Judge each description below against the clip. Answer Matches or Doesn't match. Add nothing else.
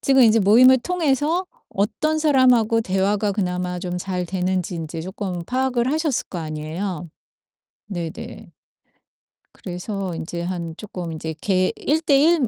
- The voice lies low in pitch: Doesn't match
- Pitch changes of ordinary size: Doesn't match